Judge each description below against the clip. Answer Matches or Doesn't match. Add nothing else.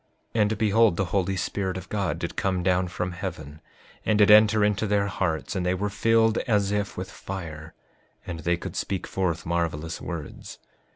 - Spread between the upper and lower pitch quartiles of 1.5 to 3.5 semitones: Matches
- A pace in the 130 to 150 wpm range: Doesn't match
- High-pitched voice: Doesn't match